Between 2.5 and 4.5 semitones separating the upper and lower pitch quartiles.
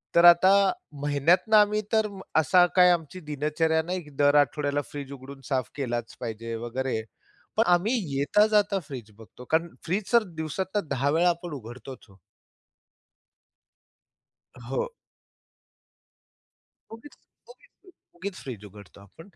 No: wide, 5.6 semitones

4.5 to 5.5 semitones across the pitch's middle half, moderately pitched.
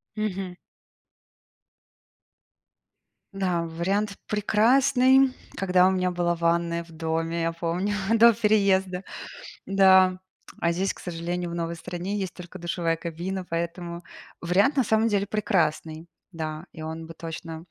No: average, 2.8 semitones; medium, 180 Hz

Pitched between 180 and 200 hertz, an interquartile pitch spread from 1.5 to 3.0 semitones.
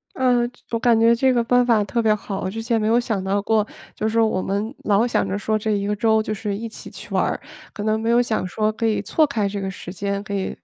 No: high, 220 Hz; narrow, 2.4 semitones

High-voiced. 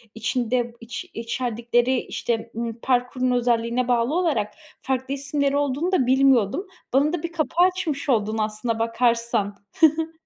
Yes: very high, 250 Hz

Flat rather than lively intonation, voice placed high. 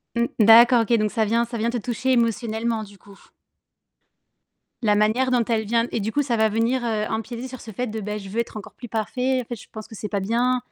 Yes: narrow, 1.9 semitones; high, 230 Hz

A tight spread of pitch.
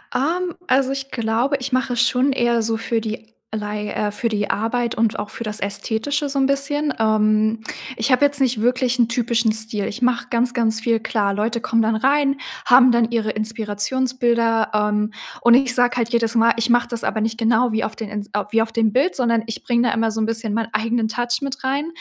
Yes: narrow, 2.3 semitones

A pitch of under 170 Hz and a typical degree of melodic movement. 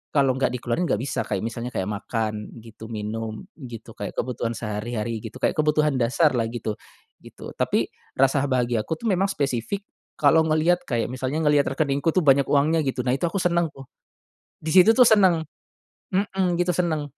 No: medium, 140 Hz; wide, 5.9 semitones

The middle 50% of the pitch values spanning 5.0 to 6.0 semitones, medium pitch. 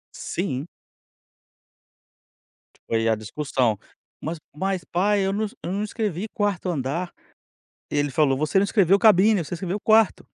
Yes: wide, 5.5 semitones; medium, 180 Hz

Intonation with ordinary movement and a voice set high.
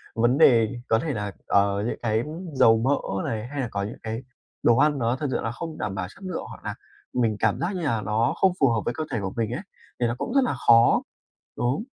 No: average, 4.2 semitones; low, 120 Hz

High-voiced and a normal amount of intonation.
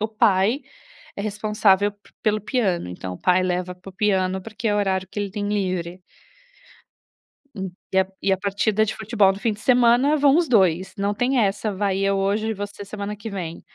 No: high, 200 Hz; narrow, 2.3 semitones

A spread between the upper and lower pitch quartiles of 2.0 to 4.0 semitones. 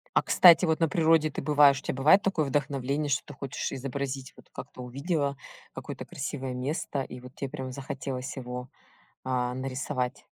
Yes: narrow, 2.4 semitones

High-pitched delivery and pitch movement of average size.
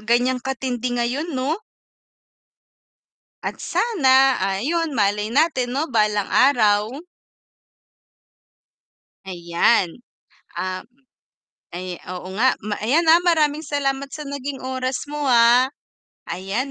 Yes: very high, 255 Hz; average, 5.0 semitones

